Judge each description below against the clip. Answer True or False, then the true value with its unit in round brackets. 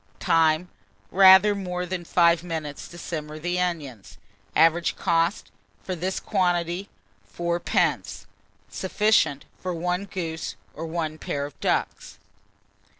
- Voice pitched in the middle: True (170 Hz)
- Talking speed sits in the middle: False (115 wpm)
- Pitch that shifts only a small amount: True (2.3 semitones)